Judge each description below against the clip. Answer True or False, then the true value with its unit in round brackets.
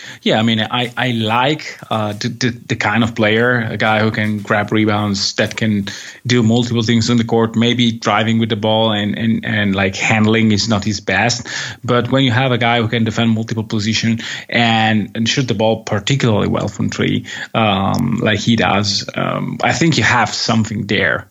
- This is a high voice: False (115 Hz)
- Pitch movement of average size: False (1.7 semitones)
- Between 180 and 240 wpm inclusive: True (200 wpm)